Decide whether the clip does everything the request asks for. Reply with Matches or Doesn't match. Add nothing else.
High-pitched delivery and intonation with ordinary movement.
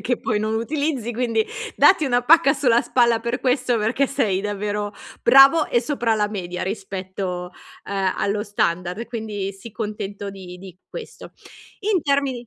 Matches